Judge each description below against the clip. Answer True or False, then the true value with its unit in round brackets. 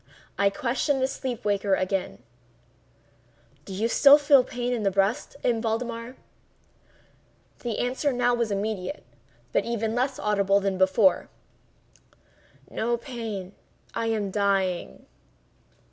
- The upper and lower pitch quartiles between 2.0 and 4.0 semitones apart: True (3.7 semitones)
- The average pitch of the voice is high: True (225 Hz)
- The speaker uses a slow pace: True (115 wpm)